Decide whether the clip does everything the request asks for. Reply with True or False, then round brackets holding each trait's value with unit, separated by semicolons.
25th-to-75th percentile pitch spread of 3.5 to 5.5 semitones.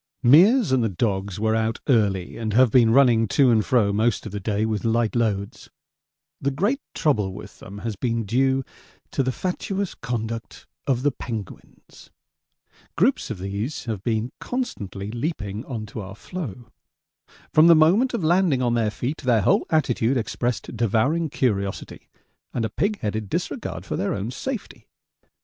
True (4.6 semitones)